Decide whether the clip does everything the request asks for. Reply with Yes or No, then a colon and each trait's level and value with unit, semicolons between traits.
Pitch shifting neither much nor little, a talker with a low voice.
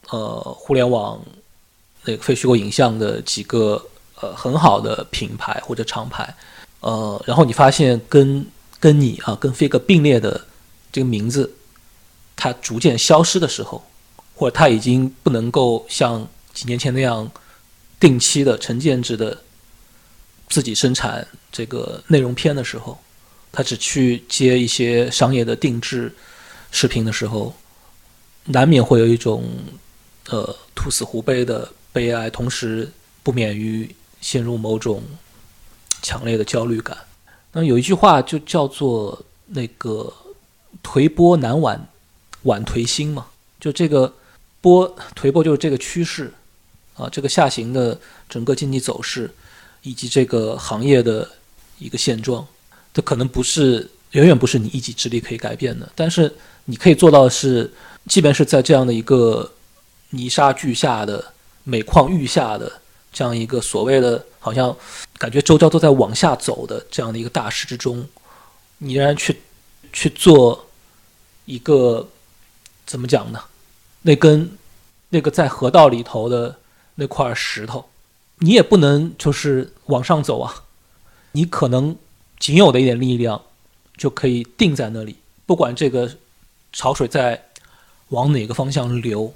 Yes: average, 4.0 semitones; low, 130 Hz